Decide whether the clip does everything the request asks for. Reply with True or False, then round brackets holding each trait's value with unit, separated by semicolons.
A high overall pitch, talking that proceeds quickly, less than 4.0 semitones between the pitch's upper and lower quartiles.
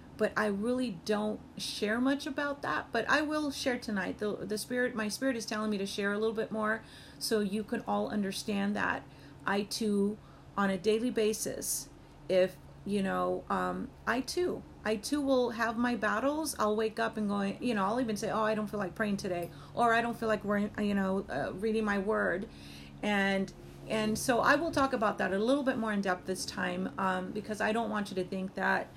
True (215 Hz; 215 wpm; 2.7 semitones)